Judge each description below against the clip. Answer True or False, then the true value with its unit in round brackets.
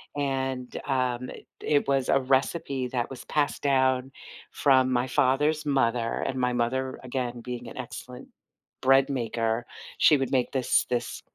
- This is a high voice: False (130 Hz)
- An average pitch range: False (1.6 semitones)